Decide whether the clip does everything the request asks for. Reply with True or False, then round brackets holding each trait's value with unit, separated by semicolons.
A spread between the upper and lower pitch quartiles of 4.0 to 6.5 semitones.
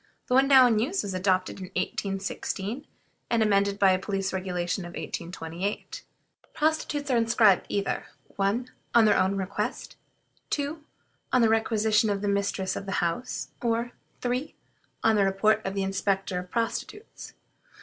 False (3.6 semitones)